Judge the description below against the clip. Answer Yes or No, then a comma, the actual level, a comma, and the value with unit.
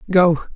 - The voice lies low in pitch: No, medium, 170 Hz